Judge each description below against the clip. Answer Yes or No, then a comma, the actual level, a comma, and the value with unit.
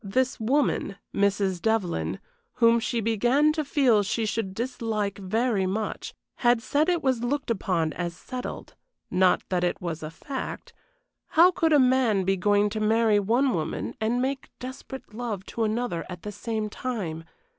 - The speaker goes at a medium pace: Yes, average, 165 wpm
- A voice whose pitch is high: Yes, high, 220 Hz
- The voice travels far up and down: No, average, 4.6 semitones